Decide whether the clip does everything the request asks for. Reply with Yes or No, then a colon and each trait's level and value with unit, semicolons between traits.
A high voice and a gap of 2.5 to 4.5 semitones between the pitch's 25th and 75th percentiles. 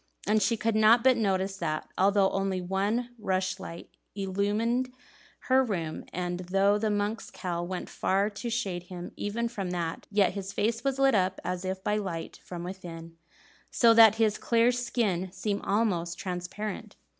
Yes: high, 200 Hz; average, 3.4 semitones